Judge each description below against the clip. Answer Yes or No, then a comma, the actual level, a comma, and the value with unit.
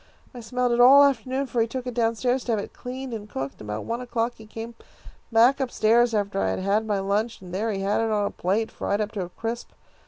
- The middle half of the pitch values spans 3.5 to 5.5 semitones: No, average, 3.0 semitones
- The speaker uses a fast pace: Yes, fast, 260 wpm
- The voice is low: No, high, 225 Hz